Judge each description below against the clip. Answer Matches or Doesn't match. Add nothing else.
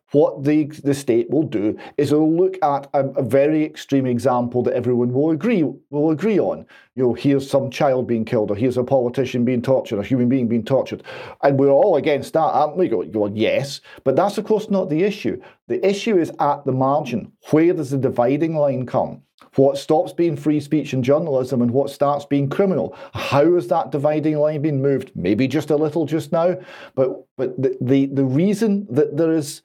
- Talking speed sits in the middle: Doesn't match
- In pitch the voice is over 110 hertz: Matches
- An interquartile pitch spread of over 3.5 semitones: Doesn't match